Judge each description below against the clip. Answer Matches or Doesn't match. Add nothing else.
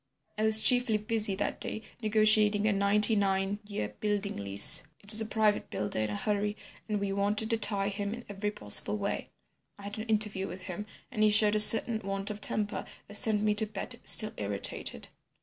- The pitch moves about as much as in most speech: Doesn't match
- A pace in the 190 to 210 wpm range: Matches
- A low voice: Doesn't match